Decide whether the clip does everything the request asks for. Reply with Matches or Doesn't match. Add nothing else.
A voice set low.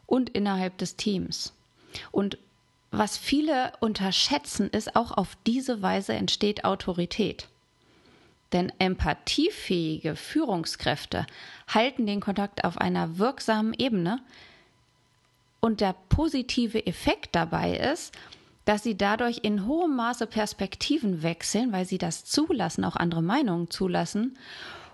Doesn't match